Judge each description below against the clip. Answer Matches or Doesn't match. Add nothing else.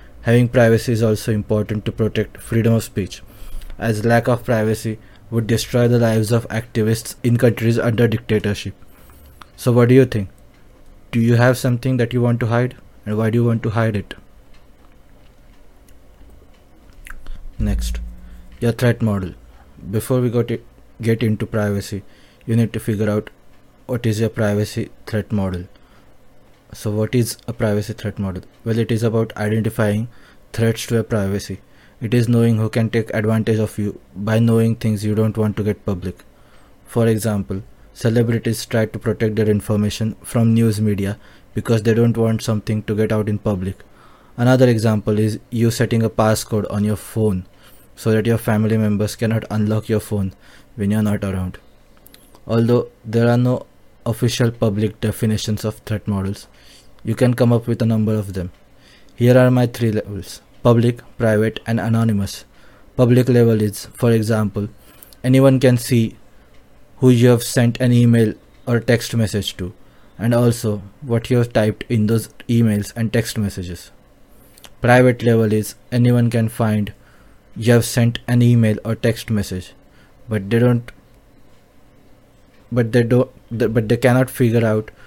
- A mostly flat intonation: Matches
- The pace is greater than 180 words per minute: Doesn't match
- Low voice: Matches